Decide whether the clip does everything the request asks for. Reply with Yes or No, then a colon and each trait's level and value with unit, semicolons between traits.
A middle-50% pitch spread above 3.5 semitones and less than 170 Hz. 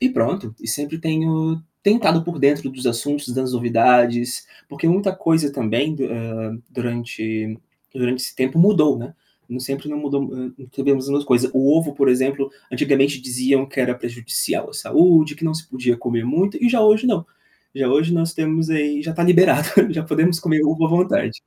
Yes: average, 4.4 semitones; medium, 140 Hz